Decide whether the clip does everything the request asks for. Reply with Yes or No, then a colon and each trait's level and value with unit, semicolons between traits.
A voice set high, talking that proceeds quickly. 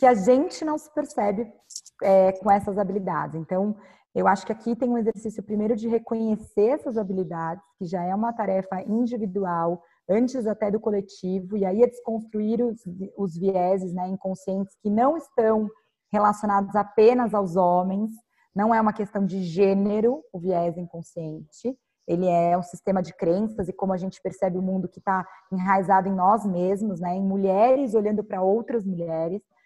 No: high, 200 Hz; average, 170 wpm